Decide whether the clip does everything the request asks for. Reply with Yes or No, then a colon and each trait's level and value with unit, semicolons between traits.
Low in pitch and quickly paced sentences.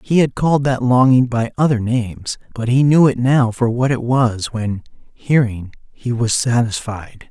No: low, 120 Hz; average, 180 wpm